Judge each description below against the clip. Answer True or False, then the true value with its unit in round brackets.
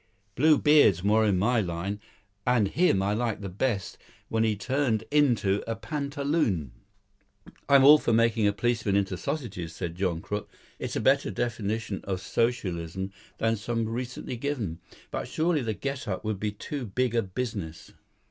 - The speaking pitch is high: False (110 Hz)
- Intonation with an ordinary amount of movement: True (4.5 semitones)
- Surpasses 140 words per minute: True (160 wpm)